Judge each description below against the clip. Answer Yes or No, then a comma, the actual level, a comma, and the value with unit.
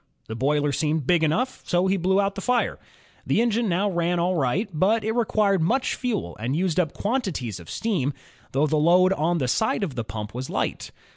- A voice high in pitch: No, medium, 175 Hz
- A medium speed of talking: No, fast, 210 wpm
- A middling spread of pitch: No, wide, 5.7 semitones